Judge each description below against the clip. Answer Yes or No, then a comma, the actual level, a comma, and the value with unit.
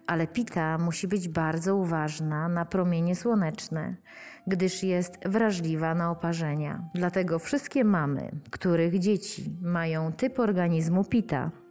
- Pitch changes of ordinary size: Yes, average, 3.0 semitones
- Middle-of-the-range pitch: Yes, medium, 175 Hz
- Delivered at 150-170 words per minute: No, average, 120 wpm